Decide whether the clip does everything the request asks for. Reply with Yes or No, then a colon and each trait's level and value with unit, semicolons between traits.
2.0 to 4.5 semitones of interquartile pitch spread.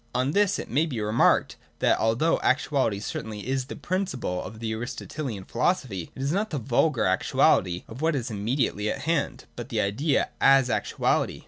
No: average, 5.2 semitones